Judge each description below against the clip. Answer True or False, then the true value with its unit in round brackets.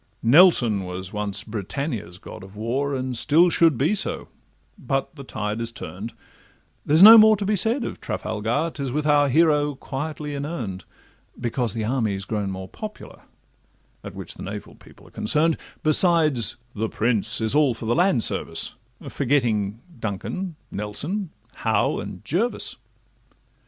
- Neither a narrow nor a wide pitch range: False (6.4 semitones)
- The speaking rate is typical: True (150 wpm)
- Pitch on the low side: True (130 Hz)